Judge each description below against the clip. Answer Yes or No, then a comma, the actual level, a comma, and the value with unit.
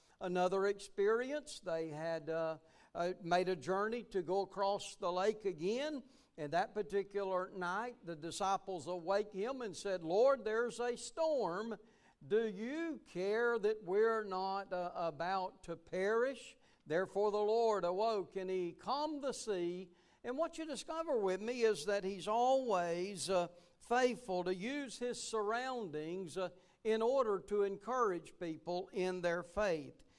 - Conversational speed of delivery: Yes, average, 145 wpm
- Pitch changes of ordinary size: Yes, average, 4.2 semitones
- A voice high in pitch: Yes, high, 200 Hz